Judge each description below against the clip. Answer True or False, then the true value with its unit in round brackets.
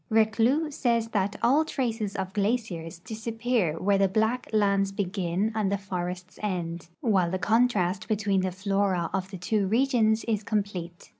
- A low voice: False (200 Hz)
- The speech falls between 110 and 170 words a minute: True (160 wpm)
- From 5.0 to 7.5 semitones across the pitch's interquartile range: False (3.2 semitones)